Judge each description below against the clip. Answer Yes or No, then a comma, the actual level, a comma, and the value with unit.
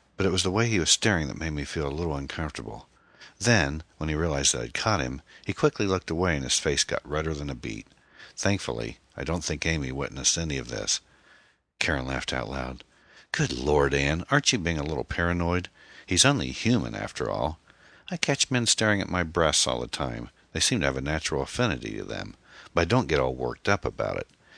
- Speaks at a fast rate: Yes, fast, 220 wpm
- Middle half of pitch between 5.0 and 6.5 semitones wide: Yes, average, 5.3 semitones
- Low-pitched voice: Yes, very low, 80 Hz